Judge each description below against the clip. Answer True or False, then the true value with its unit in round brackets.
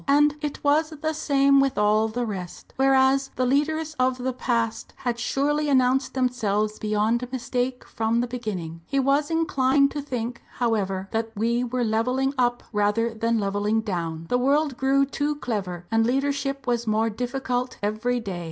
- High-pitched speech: True (245 Hz)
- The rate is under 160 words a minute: False (165 wpm)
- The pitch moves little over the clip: False (3.7 semitones)